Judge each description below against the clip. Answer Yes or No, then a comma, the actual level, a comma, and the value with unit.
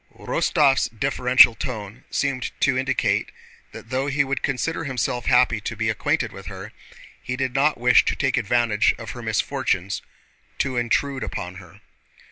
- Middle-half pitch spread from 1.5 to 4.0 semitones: Yes, average, 3.5 semitones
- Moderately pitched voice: No, low, 125 Hz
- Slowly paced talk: No, average, 155 wpm